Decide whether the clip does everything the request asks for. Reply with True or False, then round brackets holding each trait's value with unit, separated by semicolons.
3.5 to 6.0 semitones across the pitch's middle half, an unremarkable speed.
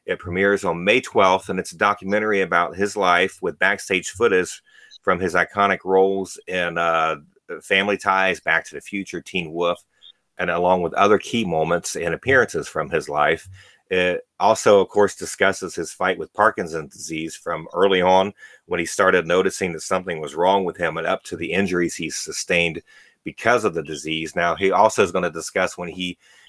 False (2.5 semitones; 190 wpm)